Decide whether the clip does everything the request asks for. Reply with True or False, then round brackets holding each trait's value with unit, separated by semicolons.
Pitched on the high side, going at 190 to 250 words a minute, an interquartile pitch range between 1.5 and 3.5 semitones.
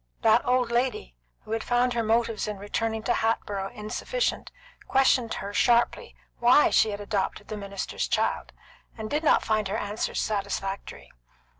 False (220 Hz; 155 wpm; 2.8 semitones)